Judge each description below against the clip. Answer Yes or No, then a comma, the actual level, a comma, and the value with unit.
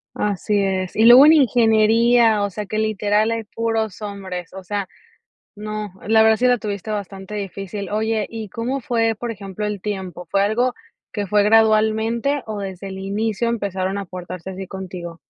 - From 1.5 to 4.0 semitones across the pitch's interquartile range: Yes, narrow, 2.5 semitones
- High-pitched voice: Yes, high, 210 Hz